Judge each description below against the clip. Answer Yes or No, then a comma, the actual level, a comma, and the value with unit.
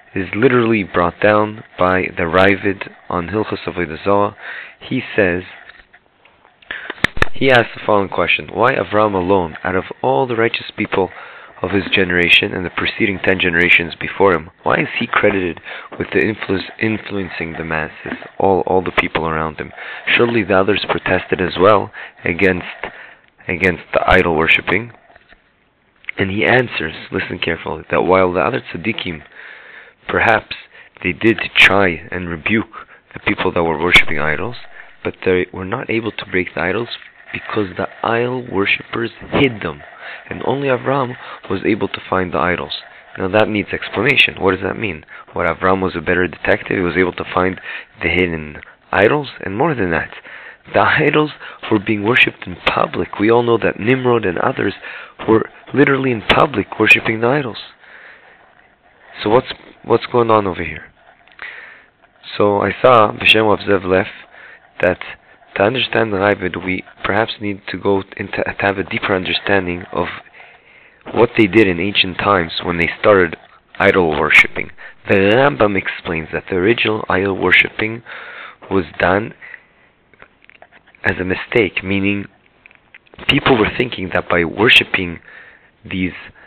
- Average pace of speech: Yes, average, 155 wpm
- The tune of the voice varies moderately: Yes, average, 3.6 semitones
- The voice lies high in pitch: No, low, 100 Hz